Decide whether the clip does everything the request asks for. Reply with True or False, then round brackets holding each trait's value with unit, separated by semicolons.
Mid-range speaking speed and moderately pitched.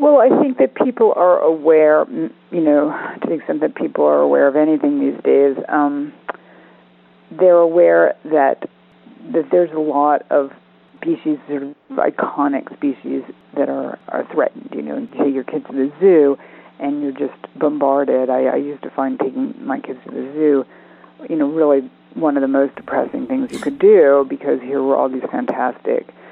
True (180 wpm; 145 Hz)